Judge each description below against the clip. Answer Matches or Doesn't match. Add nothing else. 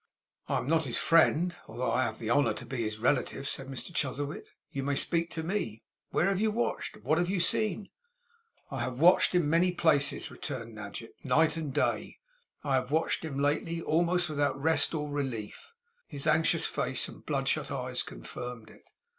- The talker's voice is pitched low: Doesn't match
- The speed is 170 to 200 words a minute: Matches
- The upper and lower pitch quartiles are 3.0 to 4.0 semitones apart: Doesn't match